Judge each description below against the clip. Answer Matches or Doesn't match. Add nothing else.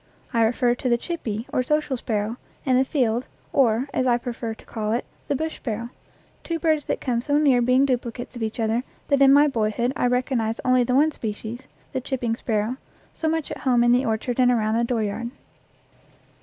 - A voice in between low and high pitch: Doesn't match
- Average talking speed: Doesn't match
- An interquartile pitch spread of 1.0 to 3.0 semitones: Matches